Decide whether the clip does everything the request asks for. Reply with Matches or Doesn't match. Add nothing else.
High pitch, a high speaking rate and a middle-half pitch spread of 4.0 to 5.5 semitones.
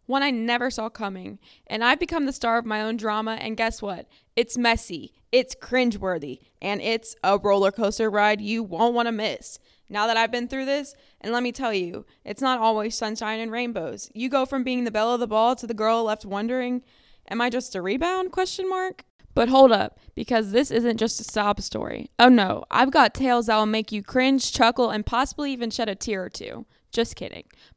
Doesn't match